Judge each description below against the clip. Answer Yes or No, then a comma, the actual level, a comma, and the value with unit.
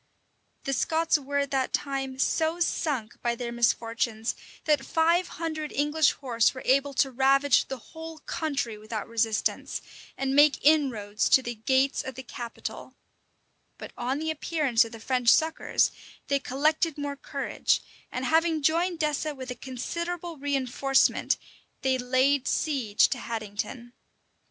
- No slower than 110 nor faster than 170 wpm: Yes, average, 145 wpm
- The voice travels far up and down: No, average, 4.0 semitones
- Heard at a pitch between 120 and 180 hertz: No, very high, 270 Hz